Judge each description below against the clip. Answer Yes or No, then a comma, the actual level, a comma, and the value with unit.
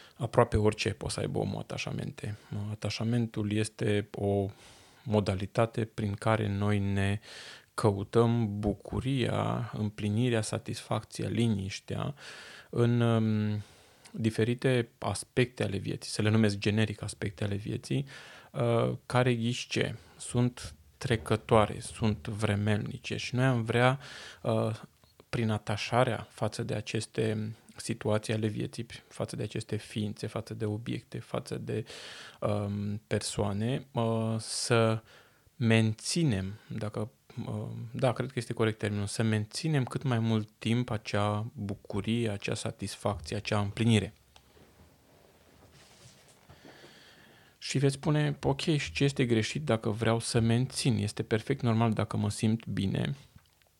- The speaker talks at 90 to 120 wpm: Yes, slow, 115 wpm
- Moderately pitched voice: No, low, 110 Hz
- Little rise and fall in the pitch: Yes, narrow, 2.1 semitones